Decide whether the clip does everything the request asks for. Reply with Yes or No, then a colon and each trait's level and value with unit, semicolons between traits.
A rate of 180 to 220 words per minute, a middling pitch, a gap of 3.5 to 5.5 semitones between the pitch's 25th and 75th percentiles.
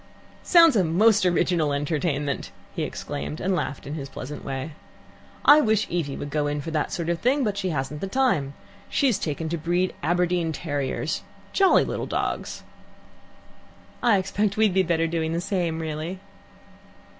No: average, 160 wpm; medium, 170 Hz; average, 4.7 semitones